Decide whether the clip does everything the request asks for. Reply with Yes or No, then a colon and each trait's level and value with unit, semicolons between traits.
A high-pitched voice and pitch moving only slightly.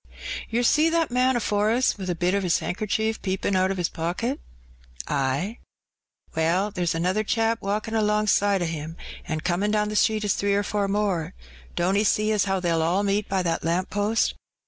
No: high, 200 Hz; average, 3.3 semitones